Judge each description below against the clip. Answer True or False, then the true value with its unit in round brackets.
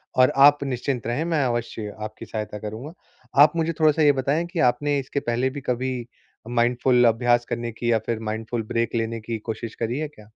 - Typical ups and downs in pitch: True (3.5 semitones)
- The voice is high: False (120 Hz)